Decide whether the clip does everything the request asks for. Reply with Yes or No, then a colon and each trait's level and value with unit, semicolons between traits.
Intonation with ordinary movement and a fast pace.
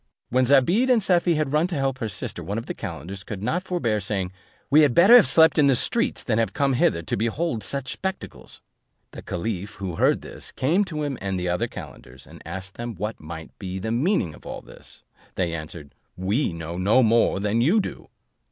No: wide, 8.2 semitones; fast, 215 wpm